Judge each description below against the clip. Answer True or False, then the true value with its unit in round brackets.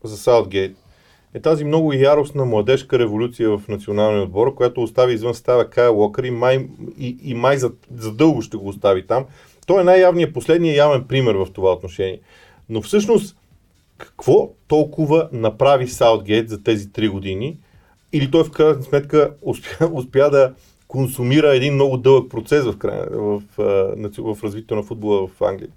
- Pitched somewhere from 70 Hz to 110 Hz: False (125 Hz)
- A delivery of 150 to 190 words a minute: True (160 wpm)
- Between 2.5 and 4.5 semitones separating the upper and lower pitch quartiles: False (5.4 semitones)